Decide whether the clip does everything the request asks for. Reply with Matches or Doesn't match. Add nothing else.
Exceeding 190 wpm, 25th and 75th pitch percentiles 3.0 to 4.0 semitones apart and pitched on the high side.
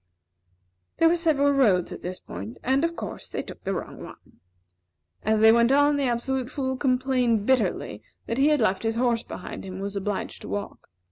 Doesn't match